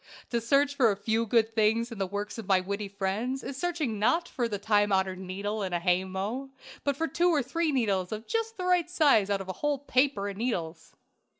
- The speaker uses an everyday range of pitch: No, wide, 5.9 semitones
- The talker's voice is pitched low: No, high, 220 Hz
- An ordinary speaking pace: No, fast, 230 wpm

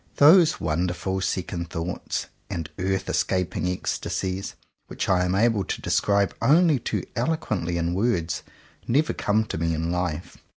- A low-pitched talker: Yes, very low, 95 Hz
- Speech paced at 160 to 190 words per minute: No, average, 145 wpm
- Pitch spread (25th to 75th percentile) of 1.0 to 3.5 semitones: No, average, 4.2 semitones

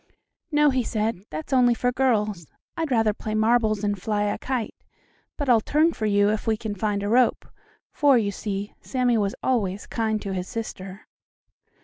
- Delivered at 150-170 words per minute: No, average, 185 wpm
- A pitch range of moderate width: Yes, average, 3.3 semitones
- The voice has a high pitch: Yes, high, 220 Hz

